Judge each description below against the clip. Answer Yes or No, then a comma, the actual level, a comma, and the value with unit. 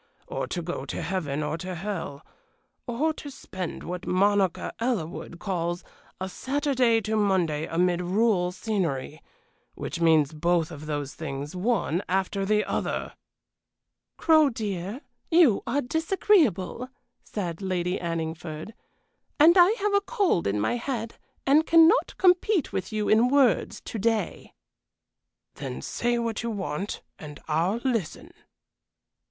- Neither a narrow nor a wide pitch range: No, wide, 6.3 semitones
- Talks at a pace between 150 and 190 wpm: No, slow, 135 wpm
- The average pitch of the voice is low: No, high, 195 Hz